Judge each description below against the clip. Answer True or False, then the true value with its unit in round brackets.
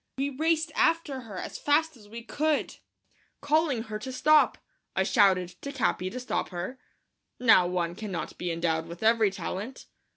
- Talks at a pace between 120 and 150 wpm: False (170 wpm)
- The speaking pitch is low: False (230 Hz)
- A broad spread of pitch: True (7.5 semitones)